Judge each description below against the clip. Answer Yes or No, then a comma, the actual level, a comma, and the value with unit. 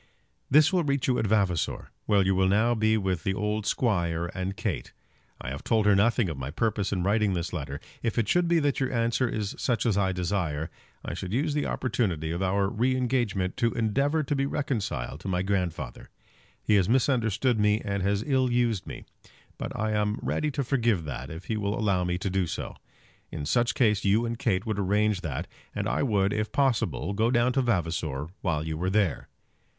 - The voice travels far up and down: No, average, 4.4 semitones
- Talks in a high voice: No, low, 105 Hz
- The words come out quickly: Yes, fast, 210 wpm